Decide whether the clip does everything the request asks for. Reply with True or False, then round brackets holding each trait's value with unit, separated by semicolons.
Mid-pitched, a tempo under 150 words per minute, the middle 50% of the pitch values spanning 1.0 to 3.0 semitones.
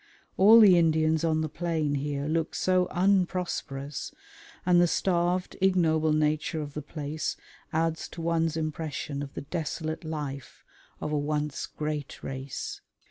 True (155 Hz; 140 wpm; 2.5 semitones)